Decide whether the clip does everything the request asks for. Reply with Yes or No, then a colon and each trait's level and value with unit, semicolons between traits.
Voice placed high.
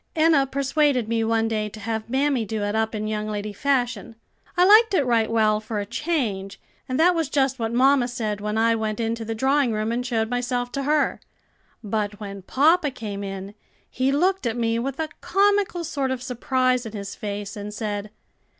Yes: high, 230 Hz